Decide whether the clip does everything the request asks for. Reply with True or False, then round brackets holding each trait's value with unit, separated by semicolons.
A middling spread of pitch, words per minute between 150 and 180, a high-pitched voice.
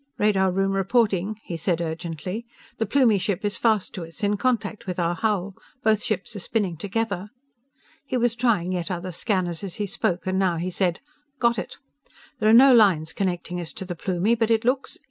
False (3.7 semitones; 200 wpm; 195 Hz)